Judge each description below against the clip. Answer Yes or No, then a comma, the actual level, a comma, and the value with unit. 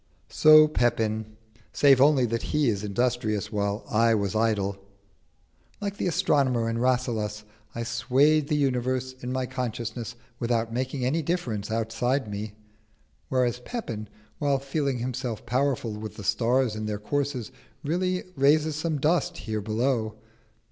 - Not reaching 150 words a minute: Yes, average, 140 wpm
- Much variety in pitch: No, average, 4.1 semitones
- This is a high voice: No, low, 125 Hz